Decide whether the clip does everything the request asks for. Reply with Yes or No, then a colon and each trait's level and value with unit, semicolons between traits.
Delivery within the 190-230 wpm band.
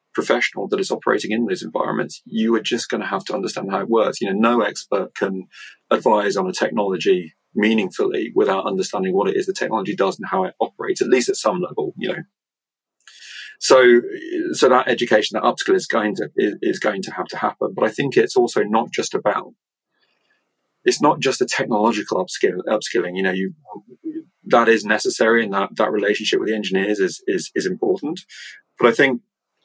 Yes: average, 200 wpm